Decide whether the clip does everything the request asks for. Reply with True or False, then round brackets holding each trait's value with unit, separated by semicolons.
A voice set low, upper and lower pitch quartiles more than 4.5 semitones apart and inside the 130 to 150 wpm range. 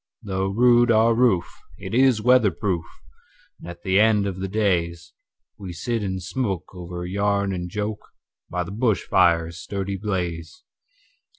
False (95 Hz; 3.7 semitones; 135 wpm)